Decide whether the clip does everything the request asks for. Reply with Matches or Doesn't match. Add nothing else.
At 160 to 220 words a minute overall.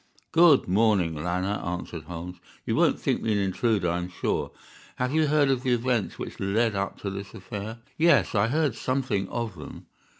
Matches